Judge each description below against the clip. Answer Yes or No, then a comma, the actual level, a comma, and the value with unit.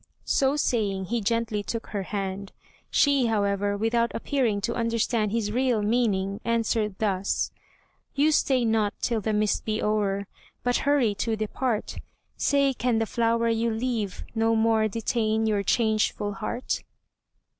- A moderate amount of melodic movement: No, narrow, 2.3 semitones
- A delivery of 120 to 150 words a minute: Yes, average, 145 wpm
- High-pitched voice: Yes, high, 225 Hz